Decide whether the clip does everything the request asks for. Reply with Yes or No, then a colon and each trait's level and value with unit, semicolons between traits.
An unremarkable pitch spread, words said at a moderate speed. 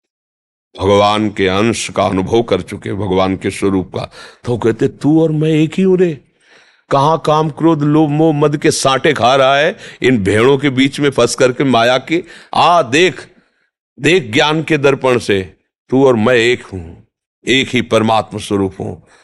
No: wide, 7.1 semitones; average, 180 wpm